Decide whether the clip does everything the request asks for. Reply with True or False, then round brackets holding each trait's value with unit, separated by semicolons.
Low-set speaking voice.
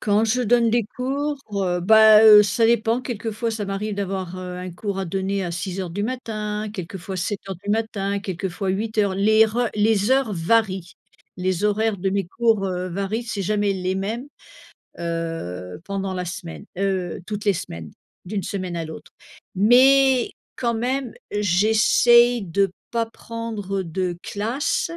False (205 Hz)